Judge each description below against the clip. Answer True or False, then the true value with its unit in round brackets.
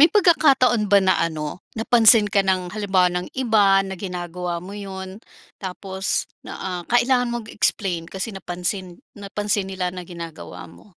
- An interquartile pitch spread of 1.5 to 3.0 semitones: False (3.5 semitones)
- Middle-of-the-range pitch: False (195 Hz)